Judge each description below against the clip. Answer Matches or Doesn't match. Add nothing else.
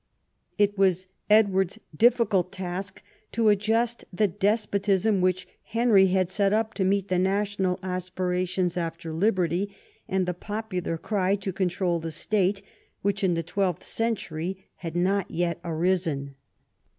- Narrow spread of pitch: Matches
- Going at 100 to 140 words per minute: Matches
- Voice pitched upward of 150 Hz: Matches